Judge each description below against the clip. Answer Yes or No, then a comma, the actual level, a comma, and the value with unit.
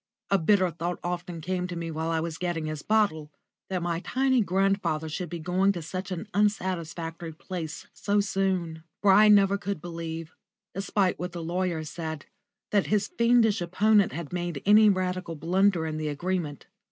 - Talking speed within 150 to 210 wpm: Yes, average, 175 wpm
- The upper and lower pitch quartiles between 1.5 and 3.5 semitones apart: Yes, average, 3.1 semitones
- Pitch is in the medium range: Yes, medium, 180 Hz